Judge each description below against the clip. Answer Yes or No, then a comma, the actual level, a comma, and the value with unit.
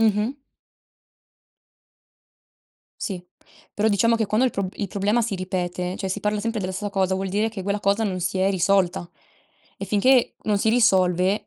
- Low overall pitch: No, high, 200 Hz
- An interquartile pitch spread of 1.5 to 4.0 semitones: Yes, narrow, 2.4 semitones